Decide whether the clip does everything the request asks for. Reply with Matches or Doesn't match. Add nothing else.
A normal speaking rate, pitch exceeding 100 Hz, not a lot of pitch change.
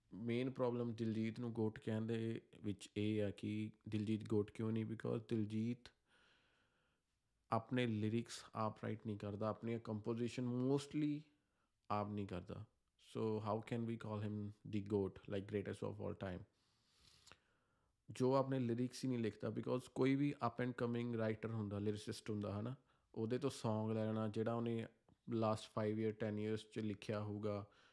Matches